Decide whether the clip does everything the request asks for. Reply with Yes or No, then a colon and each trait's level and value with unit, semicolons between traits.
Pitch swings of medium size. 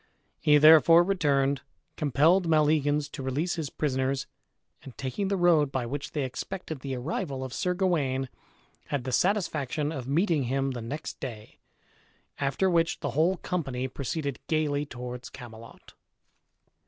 Yes: average, 3.7 semitones